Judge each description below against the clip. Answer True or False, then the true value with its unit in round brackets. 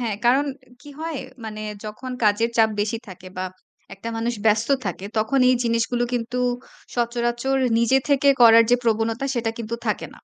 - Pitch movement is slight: True (1.9 semitones)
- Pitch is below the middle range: False (230 Hz)